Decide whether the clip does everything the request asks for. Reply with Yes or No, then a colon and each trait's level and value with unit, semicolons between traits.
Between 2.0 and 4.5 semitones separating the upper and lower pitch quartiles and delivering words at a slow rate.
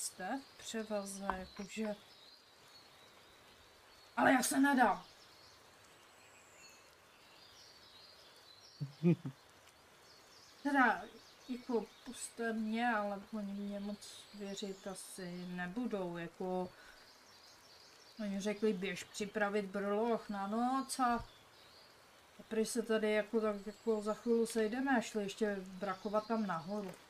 Yes: narrow, 2.5 semitones; slow, 95 wpm